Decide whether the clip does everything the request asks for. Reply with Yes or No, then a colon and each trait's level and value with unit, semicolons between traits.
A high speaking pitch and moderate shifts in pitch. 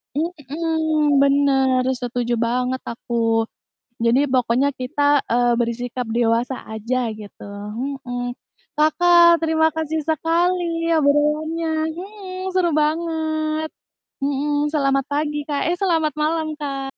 Yes: very high, 290 Hz; average, 4.1 semitones